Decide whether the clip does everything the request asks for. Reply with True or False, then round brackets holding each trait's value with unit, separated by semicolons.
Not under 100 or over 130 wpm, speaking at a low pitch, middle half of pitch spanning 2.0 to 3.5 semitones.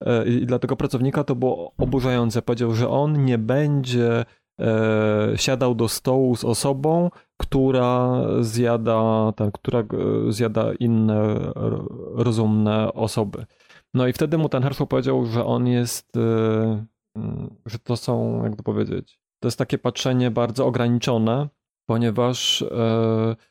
True (125 wpm; 120 Hz; 2.6 semitones)